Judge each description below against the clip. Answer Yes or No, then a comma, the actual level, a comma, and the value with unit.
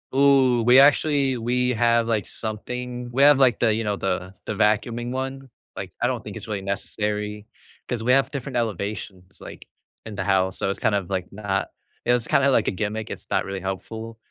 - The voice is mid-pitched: No, low, 115 Hz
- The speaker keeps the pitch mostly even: No, average, 3.6 semitones